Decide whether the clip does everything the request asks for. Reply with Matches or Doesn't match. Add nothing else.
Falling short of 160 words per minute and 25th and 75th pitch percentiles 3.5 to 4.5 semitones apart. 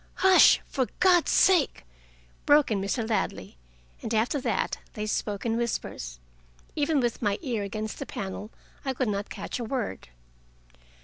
Doesn't match